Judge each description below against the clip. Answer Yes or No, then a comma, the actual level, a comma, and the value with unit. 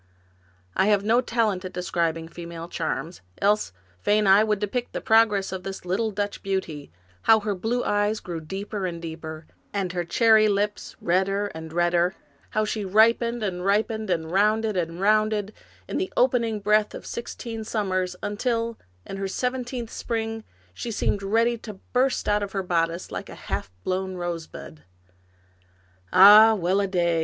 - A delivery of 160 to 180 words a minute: Yes, average, 165 wpm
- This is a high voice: Yes, high, 200 Hz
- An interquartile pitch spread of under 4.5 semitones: Yes, average, 3.4 semitones